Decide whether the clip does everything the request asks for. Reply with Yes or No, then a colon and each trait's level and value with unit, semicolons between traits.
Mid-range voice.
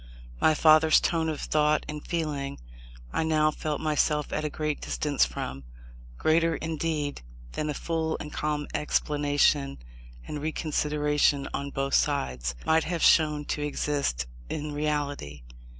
Yes: medium, 150 Hz